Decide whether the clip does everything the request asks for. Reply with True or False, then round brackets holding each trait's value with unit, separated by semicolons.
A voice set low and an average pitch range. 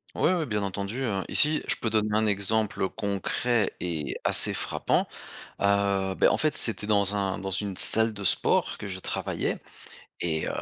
False (100 Hz; 2.2 semitones)